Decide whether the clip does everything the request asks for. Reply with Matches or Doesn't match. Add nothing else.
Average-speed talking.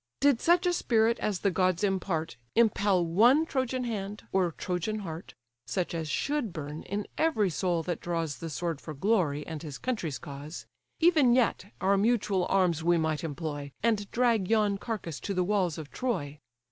Matches